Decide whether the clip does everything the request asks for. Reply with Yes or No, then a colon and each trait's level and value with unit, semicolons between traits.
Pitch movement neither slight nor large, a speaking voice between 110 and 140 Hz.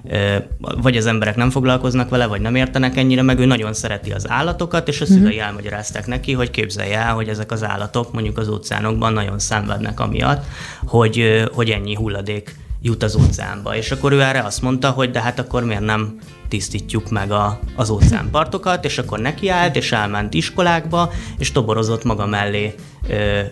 Yes: average, 3.5 semitones; low, 115 Hz